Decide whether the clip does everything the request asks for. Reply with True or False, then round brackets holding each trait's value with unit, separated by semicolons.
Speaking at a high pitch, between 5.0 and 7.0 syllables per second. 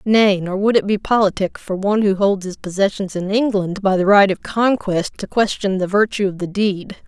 True (200 Hz; 5.1 syllables/s)